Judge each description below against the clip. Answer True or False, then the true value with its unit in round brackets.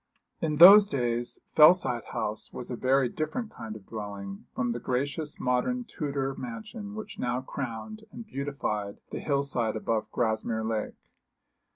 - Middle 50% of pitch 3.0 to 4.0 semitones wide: False (5.5 semitones)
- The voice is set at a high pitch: False (125 Hz)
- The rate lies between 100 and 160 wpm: True (150 wpm)